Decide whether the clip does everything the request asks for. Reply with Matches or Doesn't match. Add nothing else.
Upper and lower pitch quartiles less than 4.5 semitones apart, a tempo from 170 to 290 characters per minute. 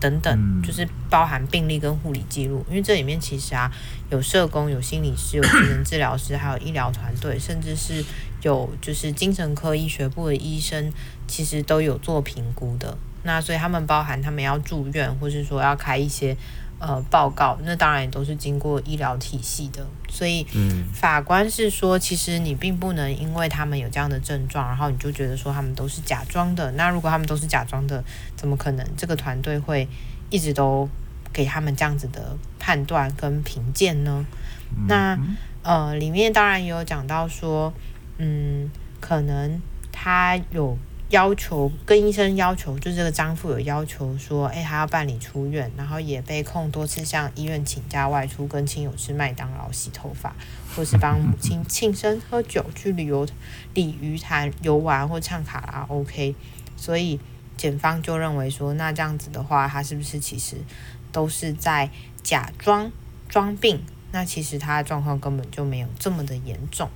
Matches